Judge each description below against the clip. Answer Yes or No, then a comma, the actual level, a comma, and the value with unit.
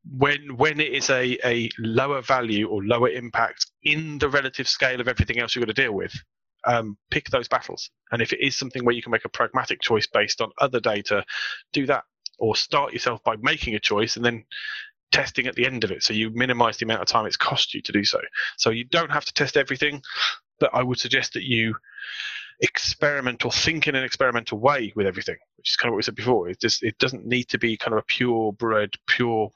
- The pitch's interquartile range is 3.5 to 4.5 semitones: Yes, average, 3.8 semitones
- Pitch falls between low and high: No, low, 125 Hz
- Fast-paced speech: Yes, fast, 240 wpm